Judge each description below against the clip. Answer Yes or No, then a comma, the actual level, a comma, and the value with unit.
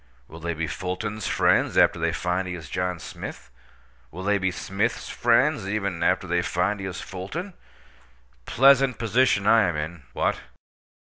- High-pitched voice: No, very low, 95 Hz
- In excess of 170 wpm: No, average, 165 wpm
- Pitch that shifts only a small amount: No, average, 3.3 semitones